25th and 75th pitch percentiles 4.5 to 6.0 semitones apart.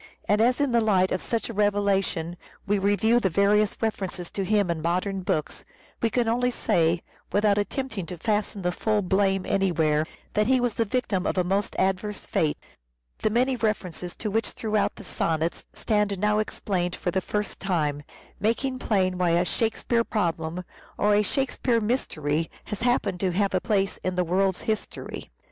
No: average, 3.2 semitones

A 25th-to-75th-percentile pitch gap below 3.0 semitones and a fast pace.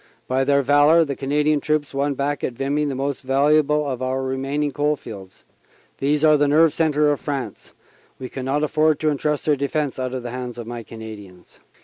Yes: narrow, 2.5 semitones; fast, 210 wpm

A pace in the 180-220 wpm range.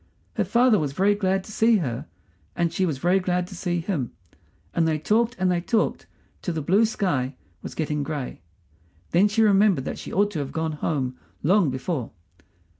Yes: average, 190 wpm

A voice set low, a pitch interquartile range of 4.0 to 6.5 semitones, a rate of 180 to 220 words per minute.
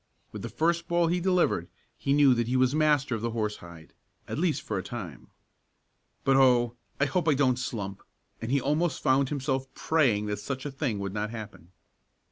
Yes: low, 130 Hz; average, 5.1 semitones; average, 195 wpm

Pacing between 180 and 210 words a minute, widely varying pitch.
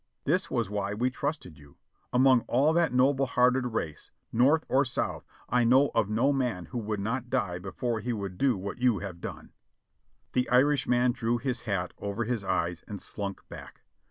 No: average, 185 wpm; average, 4.4 semitones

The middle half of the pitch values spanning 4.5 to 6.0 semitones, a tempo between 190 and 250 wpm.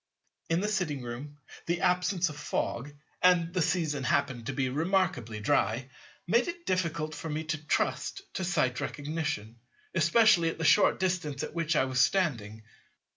No: wide, 5.5 semitones; average, 165 wpm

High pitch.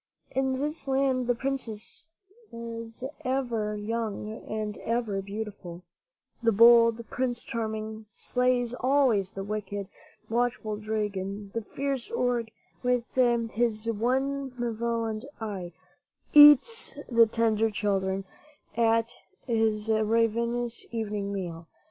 Yes: high, 230 Hz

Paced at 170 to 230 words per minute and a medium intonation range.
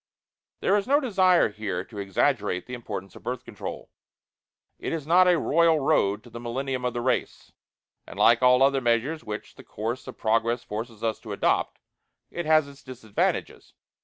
No: average, 180 wpm; wide, 5.8 semitones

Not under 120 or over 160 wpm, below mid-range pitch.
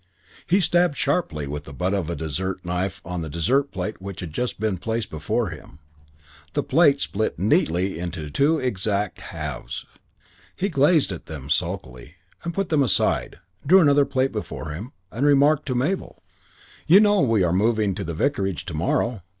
No: average, 175 wpm; low, 100 Hz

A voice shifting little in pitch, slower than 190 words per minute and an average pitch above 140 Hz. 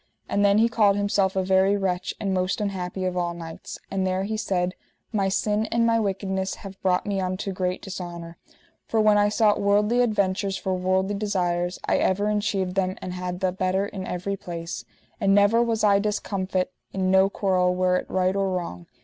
No: narrow, 1.8 semitones; average, 195 wpm; high, 190 Hz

